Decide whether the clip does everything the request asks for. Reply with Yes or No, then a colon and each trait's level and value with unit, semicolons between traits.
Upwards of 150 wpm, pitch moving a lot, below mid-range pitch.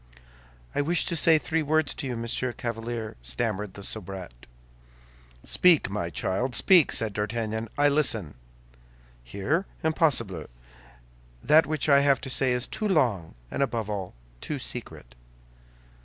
No: average, 140 wpm; wide, 6.2 semitones; low, 120 Hz